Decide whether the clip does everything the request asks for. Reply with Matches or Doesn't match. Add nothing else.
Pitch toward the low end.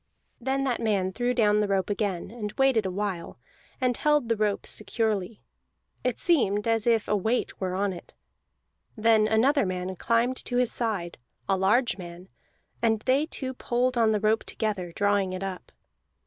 Doesn't match